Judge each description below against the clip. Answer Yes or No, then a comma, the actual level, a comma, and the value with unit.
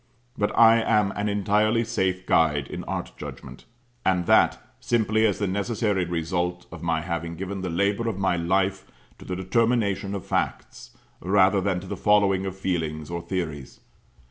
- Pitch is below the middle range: Yes, very low, 95 Hz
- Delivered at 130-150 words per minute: No, average, 165 wpm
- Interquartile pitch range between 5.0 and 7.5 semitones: No, average, 2.9 semitones